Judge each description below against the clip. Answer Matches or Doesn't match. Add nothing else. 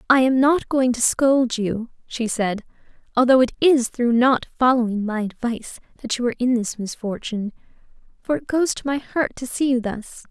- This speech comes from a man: Doesn't match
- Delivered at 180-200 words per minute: Matches